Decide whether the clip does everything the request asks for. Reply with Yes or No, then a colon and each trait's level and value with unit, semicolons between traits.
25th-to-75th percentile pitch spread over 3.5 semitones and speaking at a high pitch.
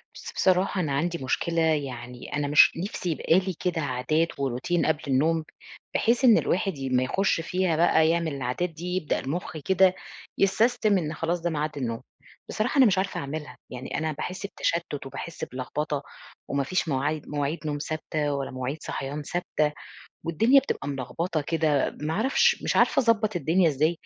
No: average, 4.2 semitones; medium, 160 Hz